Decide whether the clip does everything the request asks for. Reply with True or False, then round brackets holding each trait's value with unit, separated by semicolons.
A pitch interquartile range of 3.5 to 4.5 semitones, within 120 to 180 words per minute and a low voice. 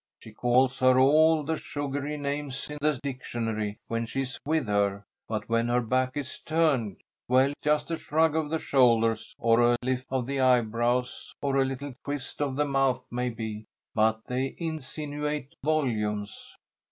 True (3.8 semitones; 165 wpm; 130 Hz)